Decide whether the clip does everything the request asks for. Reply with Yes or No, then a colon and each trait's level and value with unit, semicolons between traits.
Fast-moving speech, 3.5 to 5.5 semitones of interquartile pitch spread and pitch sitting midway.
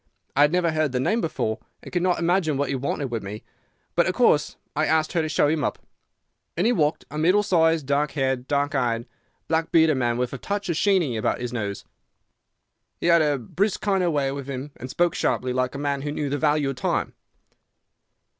Yes: fast, 225 wpm; average, 4.1 semitones; medium, 145 Hz